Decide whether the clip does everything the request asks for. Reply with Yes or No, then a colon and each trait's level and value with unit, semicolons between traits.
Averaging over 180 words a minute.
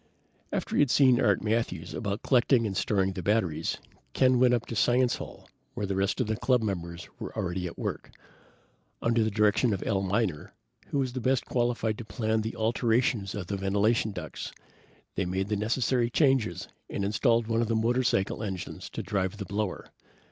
Yes: average, 190 wpm